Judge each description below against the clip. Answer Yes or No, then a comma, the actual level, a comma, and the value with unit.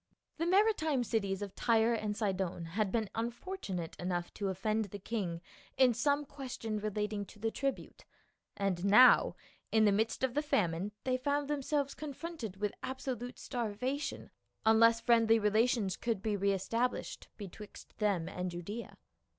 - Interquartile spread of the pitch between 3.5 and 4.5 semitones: Yes, average, 4.2 semitones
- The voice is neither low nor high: No, high, 220 Hz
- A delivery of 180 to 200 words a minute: No, average, 150 wpm